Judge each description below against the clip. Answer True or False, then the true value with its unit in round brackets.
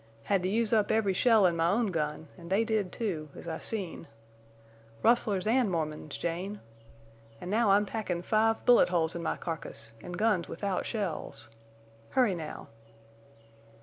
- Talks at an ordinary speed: True (160 wpm)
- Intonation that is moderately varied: True (4.5 semitones)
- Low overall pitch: False (190 Hz)